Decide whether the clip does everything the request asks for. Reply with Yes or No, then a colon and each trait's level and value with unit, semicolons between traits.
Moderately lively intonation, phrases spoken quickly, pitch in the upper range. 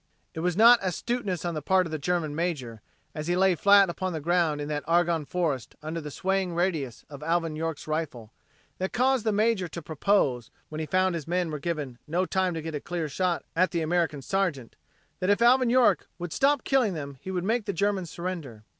No: average, 3.7 semitones; fast, 215 wpm; medium, 170 Hz